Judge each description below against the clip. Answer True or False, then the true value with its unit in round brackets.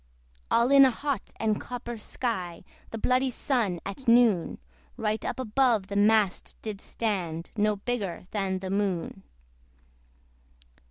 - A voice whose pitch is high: True (215 Hz)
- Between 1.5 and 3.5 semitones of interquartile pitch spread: False (3.9 semitones)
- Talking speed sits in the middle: False (130 wpm)